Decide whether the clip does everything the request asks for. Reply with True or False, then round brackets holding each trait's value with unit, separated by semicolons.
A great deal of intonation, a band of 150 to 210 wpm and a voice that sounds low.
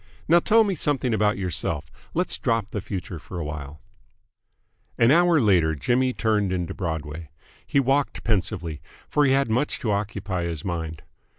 True (7.6 semitones; 160 wpm; 105 Hz)